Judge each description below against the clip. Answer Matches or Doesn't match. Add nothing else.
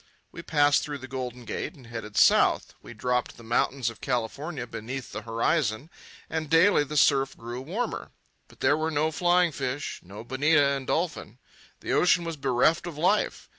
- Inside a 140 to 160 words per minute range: Doesn't match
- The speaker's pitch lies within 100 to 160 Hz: Matches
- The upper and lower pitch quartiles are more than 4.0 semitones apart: Matches